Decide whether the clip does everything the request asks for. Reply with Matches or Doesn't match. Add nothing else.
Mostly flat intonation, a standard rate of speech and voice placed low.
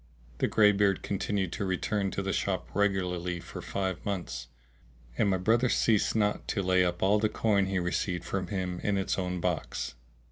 Matches